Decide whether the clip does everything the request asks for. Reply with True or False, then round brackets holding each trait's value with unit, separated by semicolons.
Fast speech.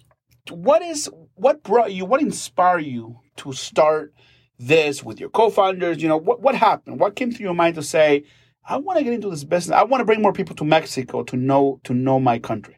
True (215 wpm)